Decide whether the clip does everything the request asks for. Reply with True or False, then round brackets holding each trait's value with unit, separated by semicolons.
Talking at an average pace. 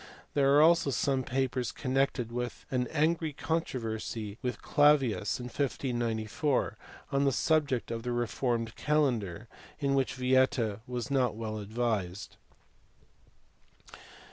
False (115 wpm)